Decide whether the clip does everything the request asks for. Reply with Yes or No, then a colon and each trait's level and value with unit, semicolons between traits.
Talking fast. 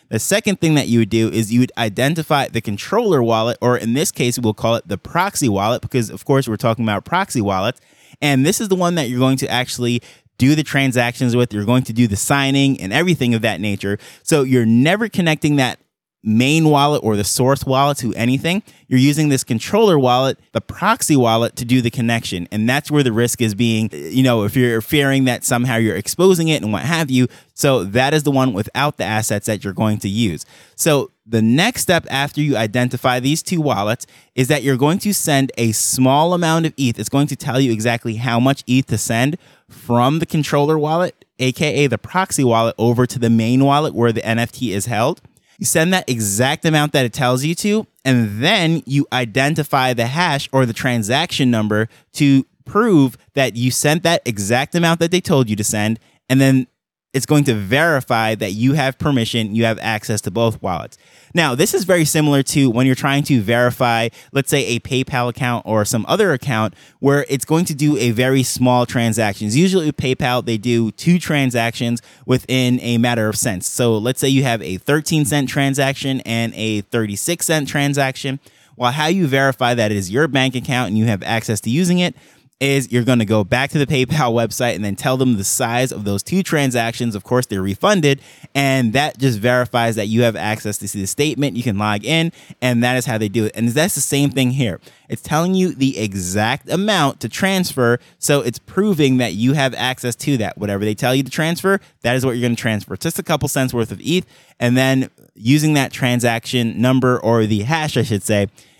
Yes: fast, 215 wpm